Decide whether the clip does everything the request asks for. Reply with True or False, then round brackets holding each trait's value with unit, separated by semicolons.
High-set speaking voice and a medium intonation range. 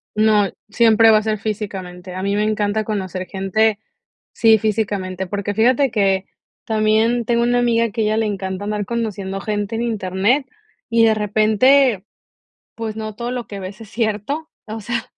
False (215 Hz; 2.2 semitones)